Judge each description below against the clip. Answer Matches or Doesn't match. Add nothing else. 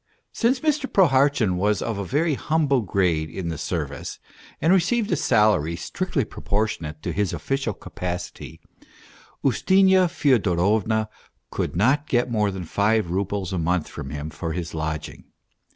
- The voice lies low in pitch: Matches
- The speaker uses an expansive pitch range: Matches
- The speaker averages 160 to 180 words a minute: Doesn't match